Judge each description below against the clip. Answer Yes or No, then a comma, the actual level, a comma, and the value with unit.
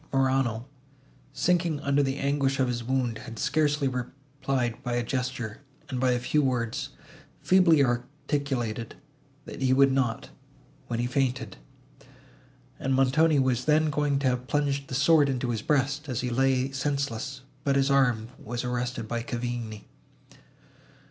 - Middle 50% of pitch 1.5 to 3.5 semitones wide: Yes, narrow, 2.5 semitones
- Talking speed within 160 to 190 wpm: No, average, 145 wpm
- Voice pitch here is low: Yes, low, 130 Hz